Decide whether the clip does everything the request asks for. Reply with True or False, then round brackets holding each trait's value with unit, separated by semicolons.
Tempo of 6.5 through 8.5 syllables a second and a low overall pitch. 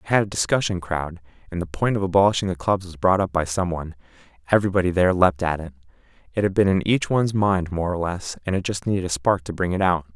True (6.8 syllables/s; 90 Hz)